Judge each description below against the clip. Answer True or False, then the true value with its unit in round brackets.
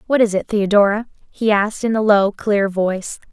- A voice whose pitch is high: True (205 Hz)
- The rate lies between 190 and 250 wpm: True (200 wpm)